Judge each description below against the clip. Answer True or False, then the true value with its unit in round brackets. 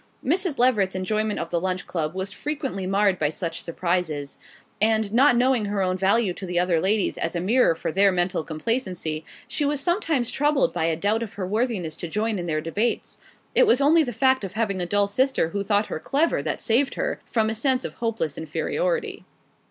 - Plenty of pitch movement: True (6.2 semitones)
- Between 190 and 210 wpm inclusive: True (205 wpm)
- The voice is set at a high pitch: True (205 Hz)